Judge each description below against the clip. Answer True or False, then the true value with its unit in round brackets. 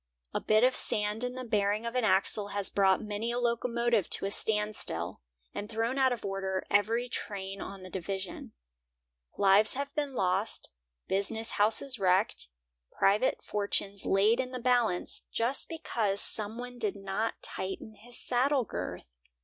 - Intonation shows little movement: False (3.5 semitones)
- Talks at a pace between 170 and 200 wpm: False (155 wpm)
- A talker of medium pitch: False (215 Hz)